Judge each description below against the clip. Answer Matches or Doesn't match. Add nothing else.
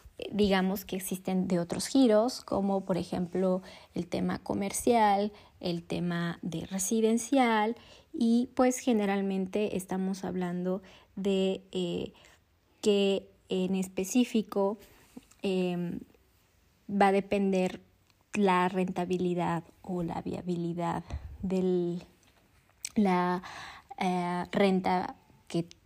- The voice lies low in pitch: Doesn't match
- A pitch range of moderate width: Doesn't match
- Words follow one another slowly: Matches